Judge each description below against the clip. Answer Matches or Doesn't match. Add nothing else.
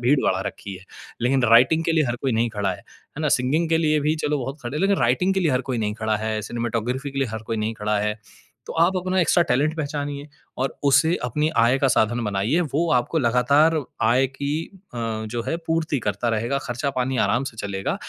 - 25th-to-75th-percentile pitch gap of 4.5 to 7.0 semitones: Matches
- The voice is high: Doesn't match